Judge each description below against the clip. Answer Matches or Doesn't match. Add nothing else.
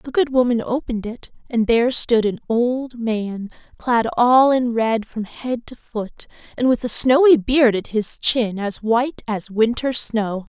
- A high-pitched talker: Matches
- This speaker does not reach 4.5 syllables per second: Matches